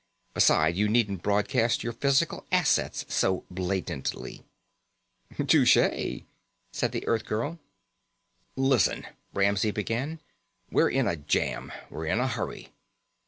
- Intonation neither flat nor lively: Yes, average, 4.6 semitones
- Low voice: Yes, low, 105 Hz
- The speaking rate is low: Yes, slow, 110 wpm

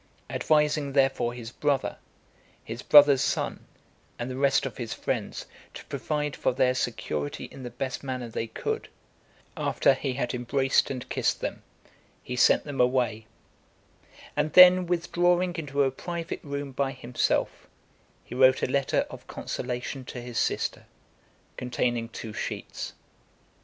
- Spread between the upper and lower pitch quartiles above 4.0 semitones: No, average, 2.9 semitones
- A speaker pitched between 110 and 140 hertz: Yes, low, 135 Hz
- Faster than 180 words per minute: No, average, 140 wpm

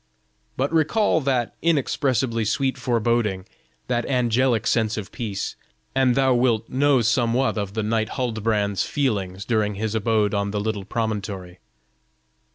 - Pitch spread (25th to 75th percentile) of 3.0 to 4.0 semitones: Yes, average, 3.5 semitones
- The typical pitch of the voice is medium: No, low, 115 Hz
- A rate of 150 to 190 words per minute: No, slow, 135 wpm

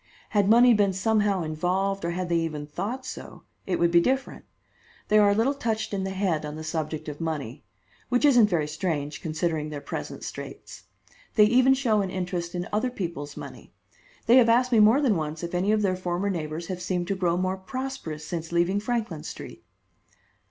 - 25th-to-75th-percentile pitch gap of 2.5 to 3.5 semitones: No, average, 4.7 semitones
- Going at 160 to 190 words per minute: No, average, 200 wpm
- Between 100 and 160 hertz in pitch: No, medium, 185 Hz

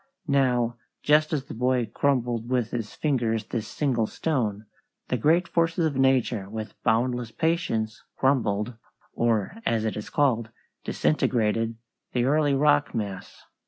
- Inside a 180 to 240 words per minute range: No, slow, 135 wpm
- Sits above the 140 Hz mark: No, low, 120 Hz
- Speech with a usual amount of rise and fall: Yes, average, 4.1 semitones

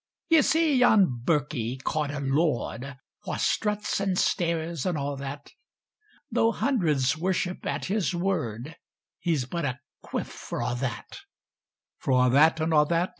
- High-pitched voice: No, medium, 160 Hz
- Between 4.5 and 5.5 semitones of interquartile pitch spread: Yes, average, 5.2 semitones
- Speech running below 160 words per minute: Yes, average, 150 wpm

